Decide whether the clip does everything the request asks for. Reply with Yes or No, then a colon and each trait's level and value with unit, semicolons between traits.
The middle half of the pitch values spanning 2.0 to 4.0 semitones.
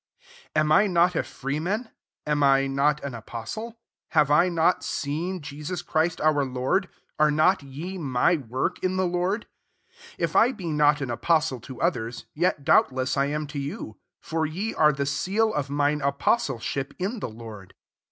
No: average, 4.5 semitones